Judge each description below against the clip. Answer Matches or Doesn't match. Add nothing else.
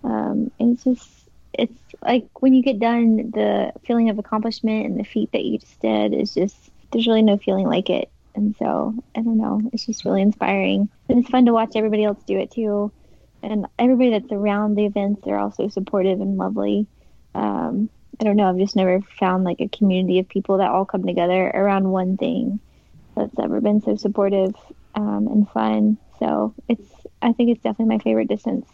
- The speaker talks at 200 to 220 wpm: Matches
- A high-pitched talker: Matches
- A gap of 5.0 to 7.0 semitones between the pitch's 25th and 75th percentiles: Doesn't match